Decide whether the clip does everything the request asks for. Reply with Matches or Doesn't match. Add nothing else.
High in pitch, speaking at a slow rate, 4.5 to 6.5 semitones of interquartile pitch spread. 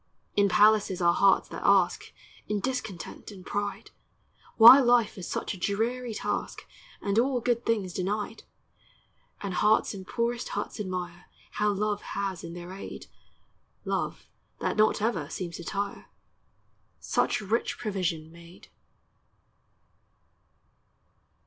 Doesn't match